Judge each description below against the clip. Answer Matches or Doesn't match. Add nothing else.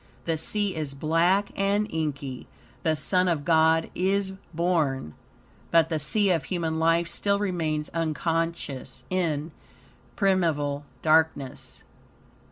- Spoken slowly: Matches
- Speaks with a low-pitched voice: Doesn't match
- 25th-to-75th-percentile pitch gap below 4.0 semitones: Matches